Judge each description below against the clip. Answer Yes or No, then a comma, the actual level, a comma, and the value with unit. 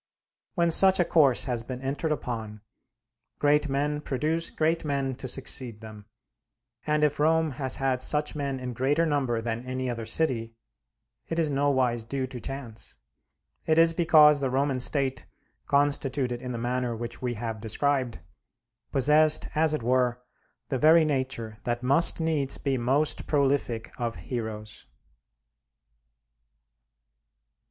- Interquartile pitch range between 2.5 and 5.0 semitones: Yes, average, 3.7 semitones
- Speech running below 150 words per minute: Yes, average, 140 wpm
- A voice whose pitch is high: No, low, 135 Hz